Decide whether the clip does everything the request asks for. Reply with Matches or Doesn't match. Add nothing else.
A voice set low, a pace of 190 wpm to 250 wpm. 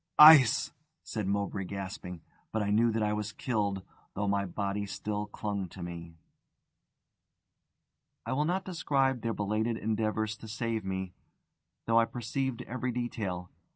Doesn't match